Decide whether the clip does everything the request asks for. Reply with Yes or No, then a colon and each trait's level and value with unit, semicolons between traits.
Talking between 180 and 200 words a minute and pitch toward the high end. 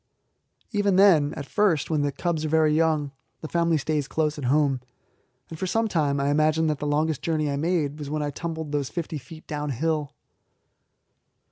No: average, 190 wpm; medium, 155 Hz